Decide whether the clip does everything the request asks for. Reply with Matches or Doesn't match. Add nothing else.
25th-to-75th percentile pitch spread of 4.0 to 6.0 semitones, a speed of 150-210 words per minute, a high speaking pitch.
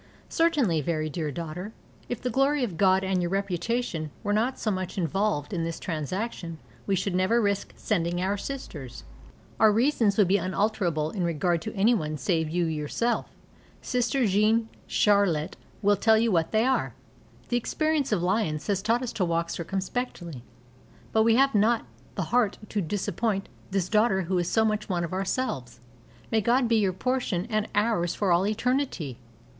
Matches